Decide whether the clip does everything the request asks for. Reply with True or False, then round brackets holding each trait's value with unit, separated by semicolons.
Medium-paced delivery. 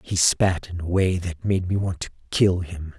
False (220 wpm)